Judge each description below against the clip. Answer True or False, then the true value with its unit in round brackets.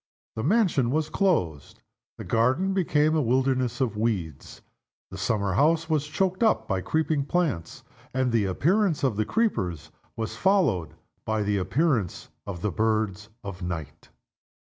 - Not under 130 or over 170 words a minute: True (145 wpm)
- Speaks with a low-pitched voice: True (120 Hz)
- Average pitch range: False (7.9 semitones)